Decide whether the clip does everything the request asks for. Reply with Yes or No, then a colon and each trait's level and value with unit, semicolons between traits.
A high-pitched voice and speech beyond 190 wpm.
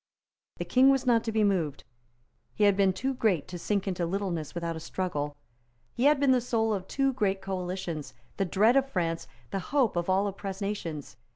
Yes: high, 195 Hz; average, 200 wpm